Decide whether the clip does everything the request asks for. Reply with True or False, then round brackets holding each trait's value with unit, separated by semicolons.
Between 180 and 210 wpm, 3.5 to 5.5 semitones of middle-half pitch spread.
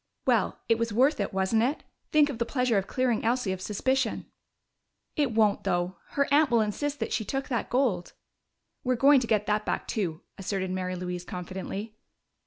True (190 wpm; 5.1 semitones)